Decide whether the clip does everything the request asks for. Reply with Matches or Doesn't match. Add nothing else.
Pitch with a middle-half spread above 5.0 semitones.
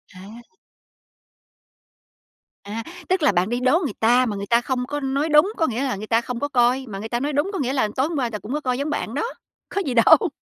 Doesn't match